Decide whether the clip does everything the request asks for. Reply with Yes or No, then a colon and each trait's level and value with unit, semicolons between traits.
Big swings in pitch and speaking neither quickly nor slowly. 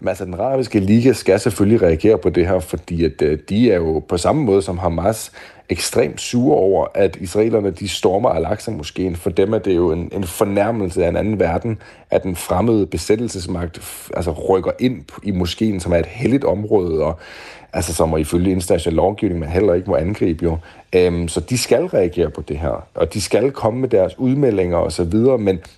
No: average, 3.7 semitones; average, 205 wpm